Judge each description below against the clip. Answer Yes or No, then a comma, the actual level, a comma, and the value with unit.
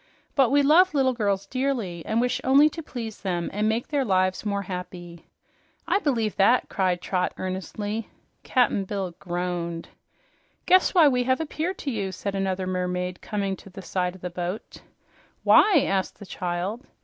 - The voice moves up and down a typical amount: No, wide, 5.8 semitones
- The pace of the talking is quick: No, average, 170 wpm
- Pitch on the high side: Yes, high, 200 Hz